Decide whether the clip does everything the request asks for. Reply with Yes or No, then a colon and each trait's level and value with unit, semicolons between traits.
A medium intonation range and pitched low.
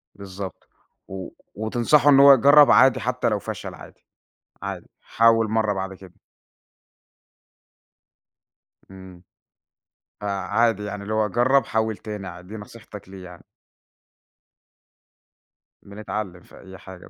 Yes: average, 3.2 semitones; low, 105 Hz